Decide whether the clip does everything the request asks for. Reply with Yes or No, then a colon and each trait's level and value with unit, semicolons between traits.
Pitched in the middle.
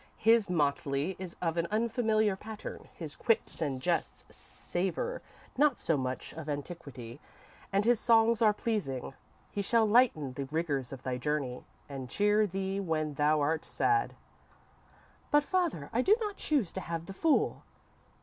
Yes: medium, 180 Hz